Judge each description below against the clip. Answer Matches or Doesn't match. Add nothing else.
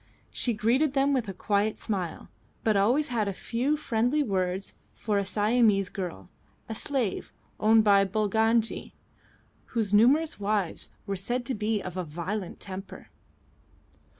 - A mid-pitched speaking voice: Doesn't match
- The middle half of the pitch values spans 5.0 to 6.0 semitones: Doesn't match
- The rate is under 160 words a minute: Matches